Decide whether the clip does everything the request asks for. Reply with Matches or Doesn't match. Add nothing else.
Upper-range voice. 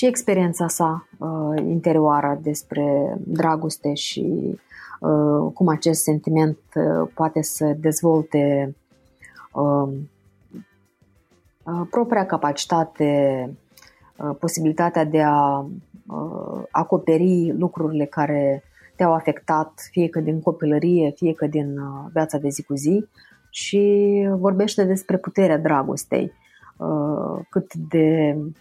Doesn't match